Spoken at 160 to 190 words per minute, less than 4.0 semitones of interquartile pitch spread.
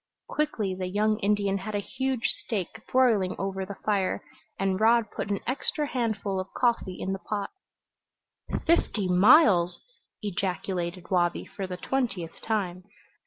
No: average, 140 wpm; average, 3.2 semitones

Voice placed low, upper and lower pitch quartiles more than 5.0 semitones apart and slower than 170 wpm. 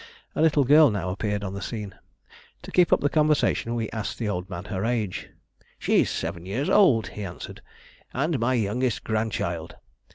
No: low, 110 Hz; wide, 5.4 semitones; average, 175 wpm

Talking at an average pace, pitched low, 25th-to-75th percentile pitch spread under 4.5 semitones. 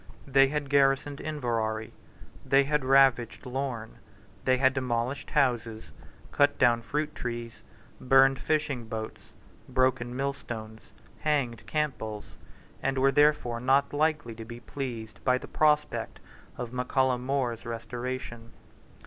No: slow, 125 wpm; low, 130 Hz; average, 2.9 semitones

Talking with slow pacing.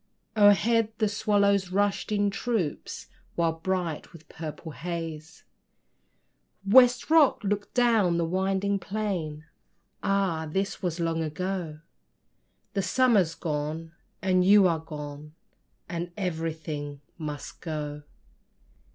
Yes: slow, 110 wpm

